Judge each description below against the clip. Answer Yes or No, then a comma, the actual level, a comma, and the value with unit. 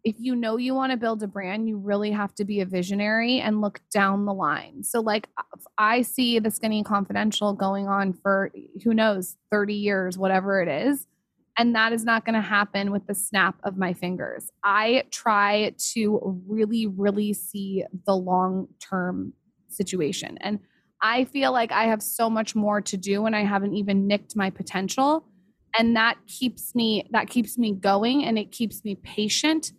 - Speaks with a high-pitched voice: Yes, high, 210 Hz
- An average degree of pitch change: No, narrow, 2.3 semitones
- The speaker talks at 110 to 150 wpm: No, average, 185 wpm